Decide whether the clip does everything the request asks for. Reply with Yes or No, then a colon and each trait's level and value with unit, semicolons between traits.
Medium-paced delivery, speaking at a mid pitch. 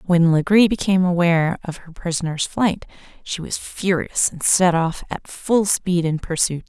Yes: average, 170 wpm; medium, 175 Hz